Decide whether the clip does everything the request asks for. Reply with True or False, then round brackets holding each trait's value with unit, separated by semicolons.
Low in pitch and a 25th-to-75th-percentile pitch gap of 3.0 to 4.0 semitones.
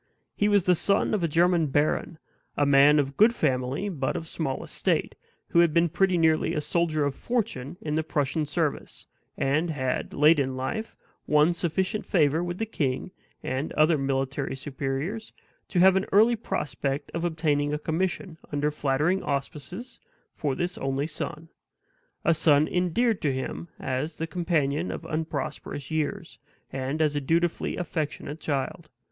False (155 Hz; 3.6 semitones)